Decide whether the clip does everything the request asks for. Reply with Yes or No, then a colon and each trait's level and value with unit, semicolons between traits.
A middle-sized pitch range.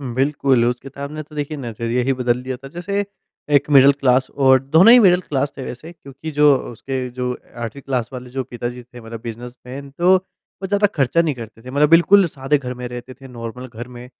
Yes: average, 3.1 semitones